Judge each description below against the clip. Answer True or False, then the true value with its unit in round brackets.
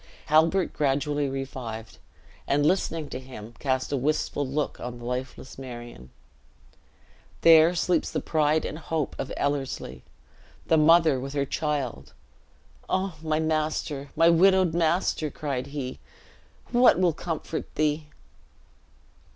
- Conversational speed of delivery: False (125 wpm)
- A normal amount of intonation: True (3.6 semitones)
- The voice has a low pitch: False (150 Hz)